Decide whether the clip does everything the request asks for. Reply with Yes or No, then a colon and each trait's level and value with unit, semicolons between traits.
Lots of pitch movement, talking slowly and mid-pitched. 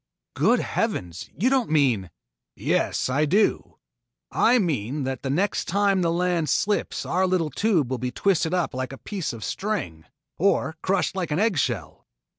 No: wide, 6.8 semitones; average, 170 wpm; medium, 165 Hz